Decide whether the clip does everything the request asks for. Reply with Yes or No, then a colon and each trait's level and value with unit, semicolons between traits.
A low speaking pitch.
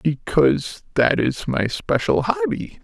Yes: low, 125 Hz